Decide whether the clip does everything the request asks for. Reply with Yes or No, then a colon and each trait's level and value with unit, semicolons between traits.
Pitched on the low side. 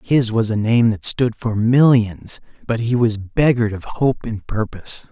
Yes: low, 115 Hz